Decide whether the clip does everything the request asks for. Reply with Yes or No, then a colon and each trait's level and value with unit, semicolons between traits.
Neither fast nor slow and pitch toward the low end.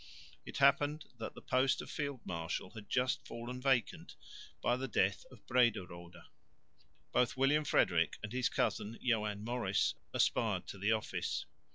Yes: average, 150 wpm; low, 120 Hz